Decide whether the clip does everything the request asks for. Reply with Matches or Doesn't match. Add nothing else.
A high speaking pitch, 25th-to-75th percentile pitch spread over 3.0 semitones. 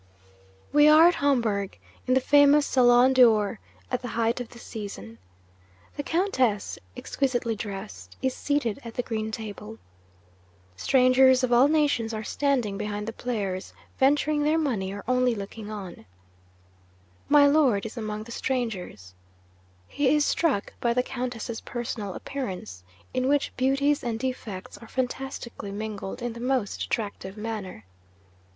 Matches